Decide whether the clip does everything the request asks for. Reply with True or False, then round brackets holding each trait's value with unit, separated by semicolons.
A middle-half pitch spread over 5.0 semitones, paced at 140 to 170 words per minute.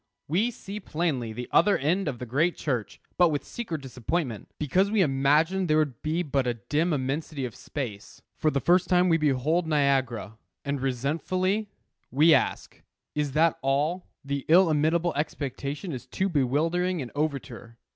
False (4.4 semitones; 160 wpm)